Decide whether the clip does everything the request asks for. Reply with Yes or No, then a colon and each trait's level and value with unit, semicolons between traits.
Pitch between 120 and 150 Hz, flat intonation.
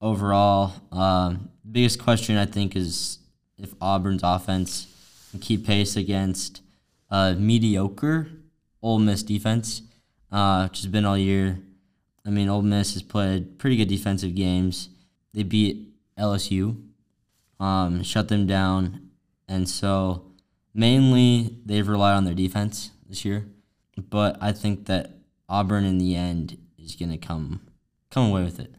No: low, 100 Hz; narrow, 1.9 semitones